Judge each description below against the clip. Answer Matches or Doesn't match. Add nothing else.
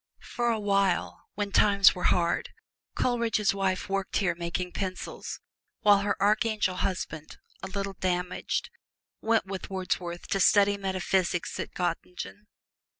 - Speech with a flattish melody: Matches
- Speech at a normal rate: Doesn't match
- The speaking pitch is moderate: Doesn't match